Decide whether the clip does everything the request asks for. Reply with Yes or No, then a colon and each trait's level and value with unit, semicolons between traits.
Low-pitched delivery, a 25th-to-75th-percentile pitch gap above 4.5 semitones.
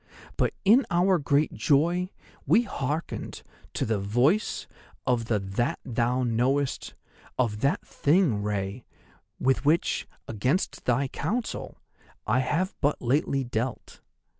Yes: low, 130 Hz; average, 5.0 semitones